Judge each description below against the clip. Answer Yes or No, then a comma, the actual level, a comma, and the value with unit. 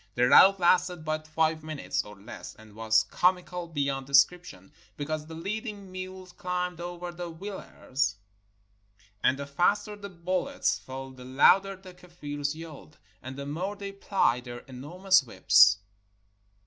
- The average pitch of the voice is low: No, medium, 165 Hz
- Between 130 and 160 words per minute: Yes, average, 150 wpm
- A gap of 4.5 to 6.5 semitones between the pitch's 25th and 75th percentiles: Yes, average, 5.2 semitones